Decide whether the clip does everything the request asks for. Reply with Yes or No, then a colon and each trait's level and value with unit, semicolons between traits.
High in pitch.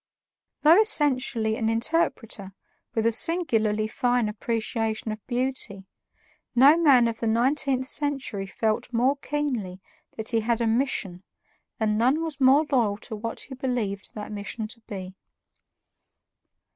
Yes: high, 230 Hz